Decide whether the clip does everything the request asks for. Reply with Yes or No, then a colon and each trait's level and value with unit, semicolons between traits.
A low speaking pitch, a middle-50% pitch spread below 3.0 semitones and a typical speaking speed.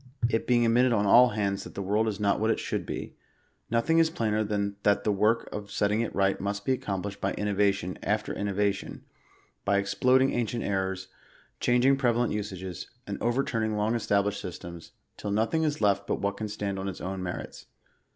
Yes: low, 105 Hz; narrow, 2.6 semitones; average, 190 wpm